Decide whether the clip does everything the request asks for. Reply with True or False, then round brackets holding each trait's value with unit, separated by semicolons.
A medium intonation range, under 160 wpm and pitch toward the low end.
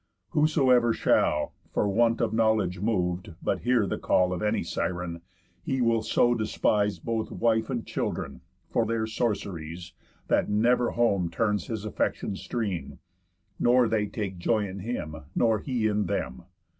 True (3.9 semitones; 150 wpm; 110 Hz)